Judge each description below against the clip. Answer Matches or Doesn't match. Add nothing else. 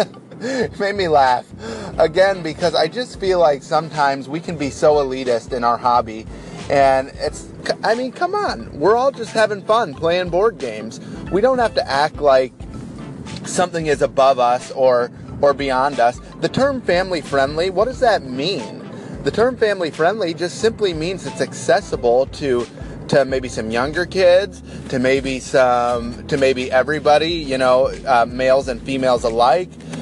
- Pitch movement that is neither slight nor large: Doesn't match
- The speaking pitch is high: Doesn't match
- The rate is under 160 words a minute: Doesn't match